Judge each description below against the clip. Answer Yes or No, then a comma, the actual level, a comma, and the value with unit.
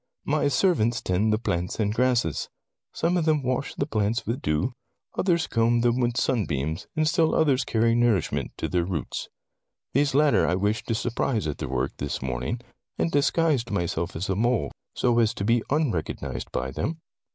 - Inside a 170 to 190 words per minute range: Yes, average, 180 wpm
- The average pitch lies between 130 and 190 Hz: No, low, 115 Hz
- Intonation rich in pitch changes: Yes, wide, 7.0 semitones